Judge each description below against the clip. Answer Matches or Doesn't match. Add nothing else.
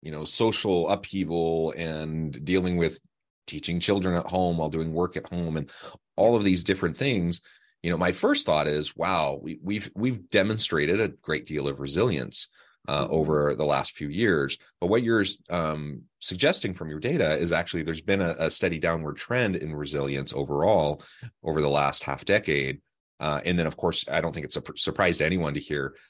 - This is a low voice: Matches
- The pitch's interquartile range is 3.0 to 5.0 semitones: Matches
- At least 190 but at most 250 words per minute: Matches